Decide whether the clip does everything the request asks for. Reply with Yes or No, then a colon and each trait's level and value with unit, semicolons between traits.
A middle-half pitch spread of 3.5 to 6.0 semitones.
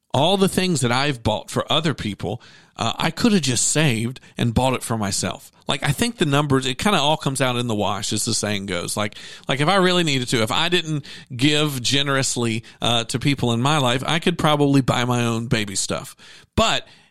Yes: average, 4.7 semitones